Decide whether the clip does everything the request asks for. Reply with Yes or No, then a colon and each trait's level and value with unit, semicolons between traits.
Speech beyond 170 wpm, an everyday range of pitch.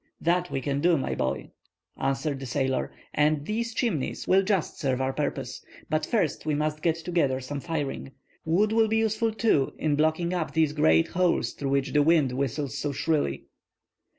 Yes: average, 180 wpm; average, 4.4 semitones